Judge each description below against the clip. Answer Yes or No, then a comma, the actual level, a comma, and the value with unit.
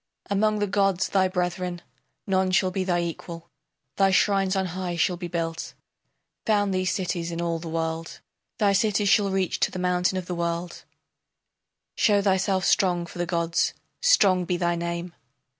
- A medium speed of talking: Yes, average, 170 wpm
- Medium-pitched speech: Yes, medium, 180 Hz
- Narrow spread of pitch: Yes, narrow, 2.1 semitones